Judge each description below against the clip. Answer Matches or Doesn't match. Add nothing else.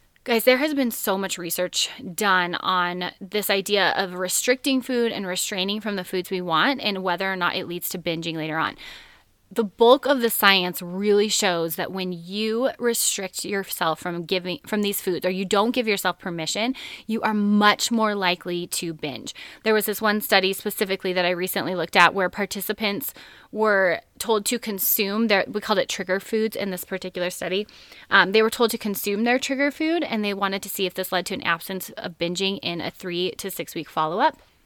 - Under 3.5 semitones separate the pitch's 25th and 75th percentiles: Matches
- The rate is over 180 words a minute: Matches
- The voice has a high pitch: Matches